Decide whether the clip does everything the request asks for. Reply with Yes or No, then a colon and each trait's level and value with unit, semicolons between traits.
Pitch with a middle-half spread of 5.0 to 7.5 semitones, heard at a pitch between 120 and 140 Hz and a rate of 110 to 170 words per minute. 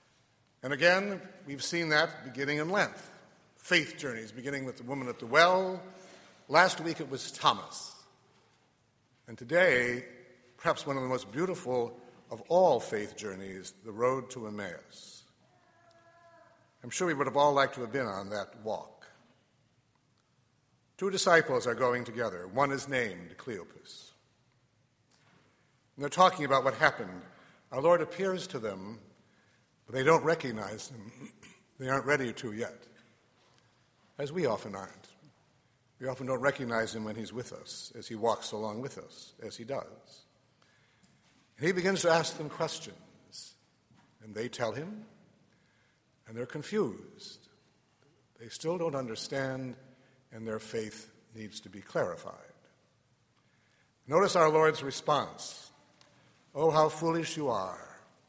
Yes: average, 5.3 semitones; low, 135 Hz; average, 140 wpm